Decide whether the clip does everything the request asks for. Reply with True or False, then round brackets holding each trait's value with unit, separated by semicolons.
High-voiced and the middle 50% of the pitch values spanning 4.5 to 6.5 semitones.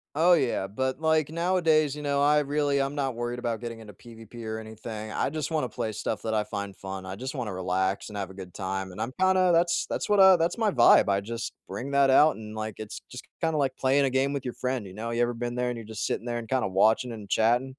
False (120 Hz; 4.8 semitones)